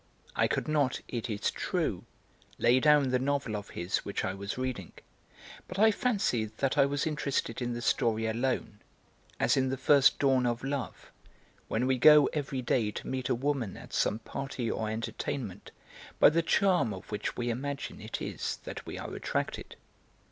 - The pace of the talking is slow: No, average, 180 wpm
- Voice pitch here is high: No, low, 130 Hz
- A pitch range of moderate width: Yes, average, 3.8 semitones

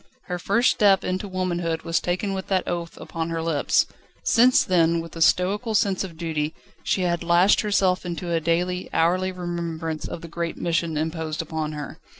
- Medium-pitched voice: Yes, medium, 170 Hz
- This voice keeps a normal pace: Yes, average, 180 wpm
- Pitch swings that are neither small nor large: No, narrow, 2.1 semitones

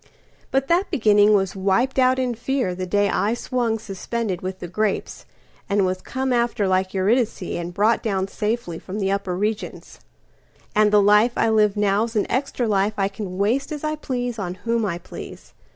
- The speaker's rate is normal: Yes, average, 170 wpm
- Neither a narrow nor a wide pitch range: Yes, average, 3.5 semitones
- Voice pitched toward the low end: No, high, 210 Hz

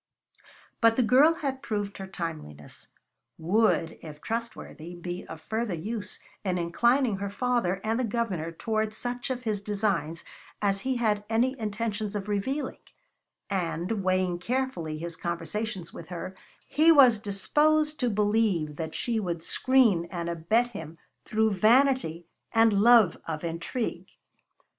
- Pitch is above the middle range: Yes, high, 210 Hz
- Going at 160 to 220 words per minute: No, average, 140 wpm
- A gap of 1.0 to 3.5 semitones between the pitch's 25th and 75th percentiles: No, wide, 5.5 semitones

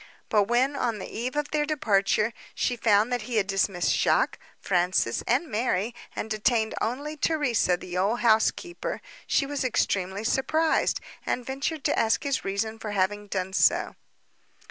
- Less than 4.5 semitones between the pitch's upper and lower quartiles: No, average, 4.9 semitones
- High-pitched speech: Yes, high, 225 Hz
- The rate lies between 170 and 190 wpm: No, average, 160 wpm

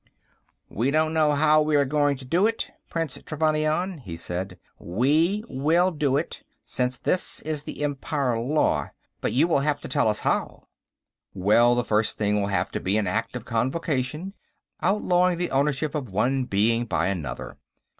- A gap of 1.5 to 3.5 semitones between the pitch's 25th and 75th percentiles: No, average, 5.3 semitones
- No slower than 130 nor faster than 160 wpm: No, average, 175 wpm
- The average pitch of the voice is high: No, medium, 140 Hz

